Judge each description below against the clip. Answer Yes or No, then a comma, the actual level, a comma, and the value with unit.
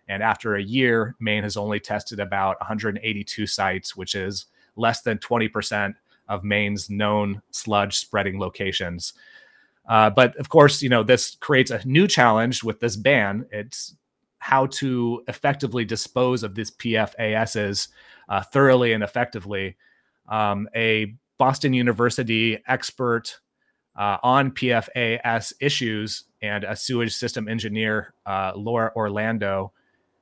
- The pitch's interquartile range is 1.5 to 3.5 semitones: Yes, average, 2.9 semitones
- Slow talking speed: Yes, slow, 130 wpm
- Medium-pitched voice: No, low, 110 Hz